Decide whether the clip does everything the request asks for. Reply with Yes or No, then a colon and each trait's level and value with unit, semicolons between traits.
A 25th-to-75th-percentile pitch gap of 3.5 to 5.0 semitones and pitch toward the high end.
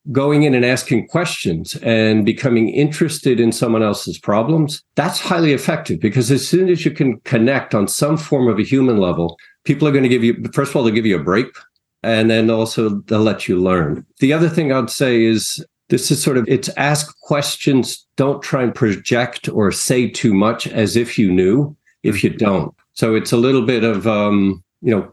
No: average, 4.6 semitones; low, 125 Hz